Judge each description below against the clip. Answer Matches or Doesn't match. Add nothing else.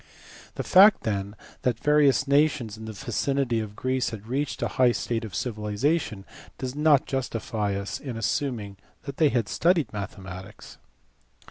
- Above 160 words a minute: Doesn't match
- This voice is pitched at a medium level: Doesn't match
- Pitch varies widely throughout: Doesn't match